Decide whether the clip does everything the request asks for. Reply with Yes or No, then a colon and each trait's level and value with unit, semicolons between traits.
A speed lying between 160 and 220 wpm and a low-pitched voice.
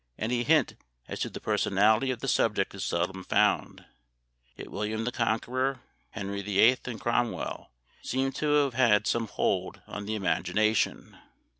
No: average, 150 wpm; low, 110 Hz